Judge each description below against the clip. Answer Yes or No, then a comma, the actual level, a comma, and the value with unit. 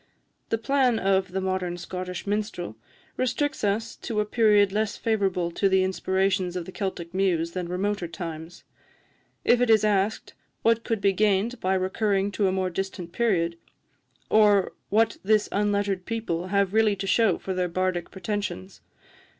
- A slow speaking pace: No, average, 160 wpm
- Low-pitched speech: No, high, 195 Hz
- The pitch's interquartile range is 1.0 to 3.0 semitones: Yes, average, 2.7 semitones